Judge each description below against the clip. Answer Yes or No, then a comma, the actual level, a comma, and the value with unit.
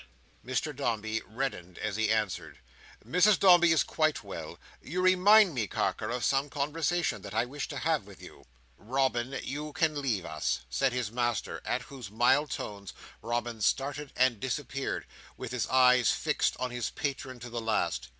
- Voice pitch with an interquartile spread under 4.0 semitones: No, average, 4.4 semitones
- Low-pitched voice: Yes, low, 130 Hz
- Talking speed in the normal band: Yes, average, 170 wpm